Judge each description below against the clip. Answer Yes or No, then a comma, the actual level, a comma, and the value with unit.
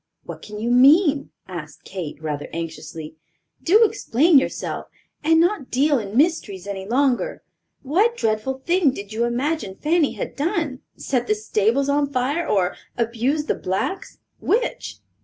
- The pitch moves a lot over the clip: Yes, wide, 7.1 semitones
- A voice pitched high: Yes, very high, 260 Hz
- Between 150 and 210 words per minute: No, average, 140 wpm